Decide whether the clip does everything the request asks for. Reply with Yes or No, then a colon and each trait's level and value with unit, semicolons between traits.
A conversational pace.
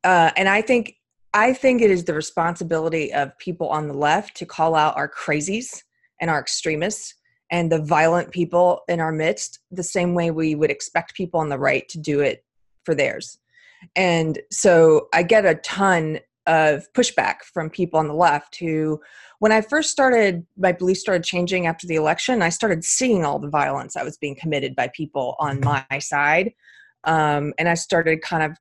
Yes: average, 190 wpm